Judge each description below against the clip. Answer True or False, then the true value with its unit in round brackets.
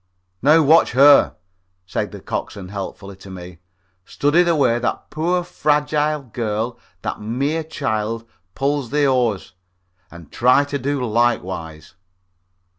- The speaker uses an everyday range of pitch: False (5.7 semitones)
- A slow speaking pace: True (125 wpm)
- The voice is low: True (125 Hz)